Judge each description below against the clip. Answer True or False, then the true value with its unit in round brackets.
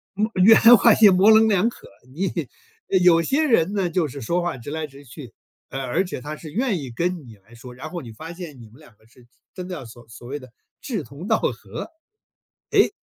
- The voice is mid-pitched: True (160 Hz)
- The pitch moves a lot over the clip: True (6.6 semitones)